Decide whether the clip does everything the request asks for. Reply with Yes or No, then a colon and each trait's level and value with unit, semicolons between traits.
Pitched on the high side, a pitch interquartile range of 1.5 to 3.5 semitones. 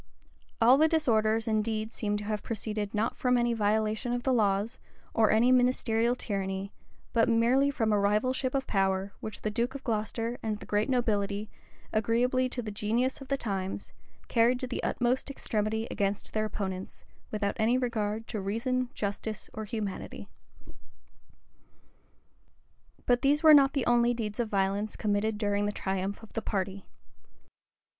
Yes: high, 220 Hz; average, 2.9 semitones